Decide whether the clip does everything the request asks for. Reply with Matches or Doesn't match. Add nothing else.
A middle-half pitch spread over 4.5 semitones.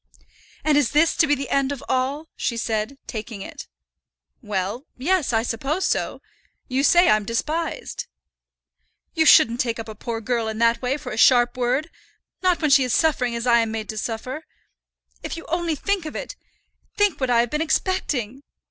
Matches